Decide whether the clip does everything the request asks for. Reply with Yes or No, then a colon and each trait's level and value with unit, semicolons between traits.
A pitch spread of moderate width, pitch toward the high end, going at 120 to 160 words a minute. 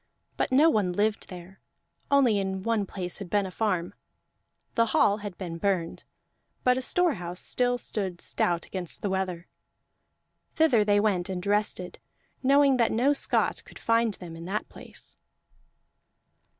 Yes: average, 4.2 semitones; high, 205 Hz; average, 150 wpm